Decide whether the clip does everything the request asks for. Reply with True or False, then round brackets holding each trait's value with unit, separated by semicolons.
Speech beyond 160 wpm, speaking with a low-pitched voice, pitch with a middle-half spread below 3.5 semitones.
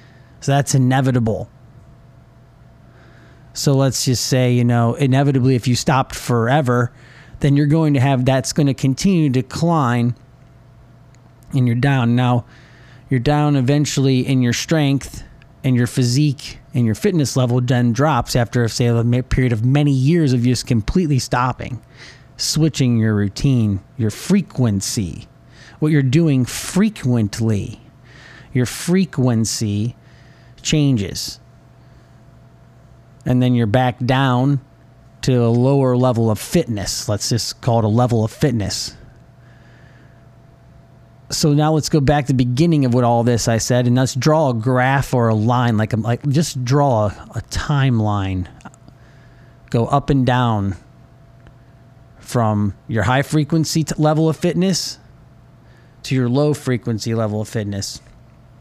False (135 wpm; 130 Hz; 2.7 semitones)